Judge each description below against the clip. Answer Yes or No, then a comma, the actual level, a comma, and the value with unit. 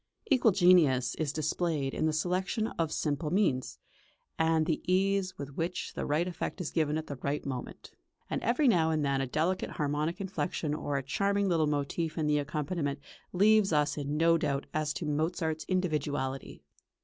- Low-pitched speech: No, medium, 155 Hz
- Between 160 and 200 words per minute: Yes, average, 175 wpm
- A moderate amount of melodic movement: Yes, average, 3.6 semitones